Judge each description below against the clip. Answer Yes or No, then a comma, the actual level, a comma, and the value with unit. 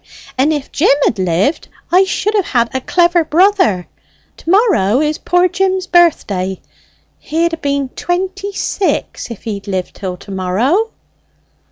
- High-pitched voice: Yes, very high, 310 Hz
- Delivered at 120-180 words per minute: Yes, average, 150 wpm